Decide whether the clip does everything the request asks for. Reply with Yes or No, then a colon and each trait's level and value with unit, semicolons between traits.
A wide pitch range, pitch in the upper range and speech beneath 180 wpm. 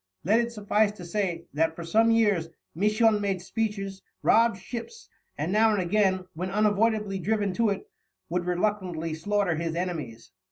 No: average, 3.6 semitones; high, 195 Hz; average, 160 wpm